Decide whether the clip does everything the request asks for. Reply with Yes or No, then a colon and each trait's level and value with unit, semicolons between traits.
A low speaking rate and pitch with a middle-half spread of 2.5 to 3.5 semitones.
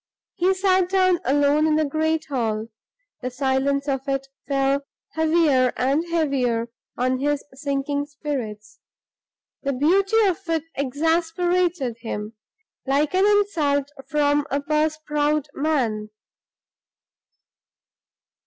Yes: slow, 110 wpm; average, 3.1 semitones